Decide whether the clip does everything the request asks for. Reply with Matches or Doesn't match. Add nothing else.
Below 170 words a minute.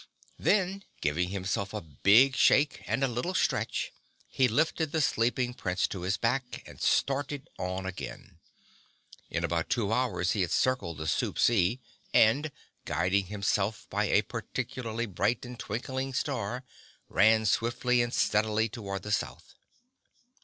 Matches